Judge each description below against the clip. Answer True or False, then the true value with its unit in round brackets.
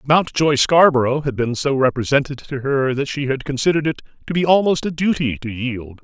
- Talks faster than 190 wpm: True (200 wpm)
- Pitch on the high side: False (140 Hz)